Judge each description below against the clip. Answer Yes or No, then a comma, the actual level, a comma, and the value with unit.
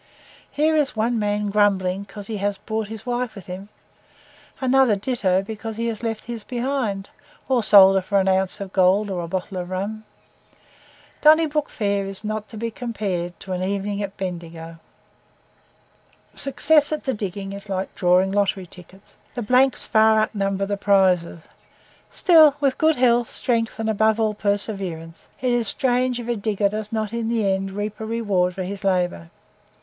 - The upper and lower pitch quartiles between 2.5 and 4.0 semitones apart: Yes, average, 3.3 semitones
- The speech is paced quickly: No, average, 175 wpm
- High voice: Yes, high, 205 Hz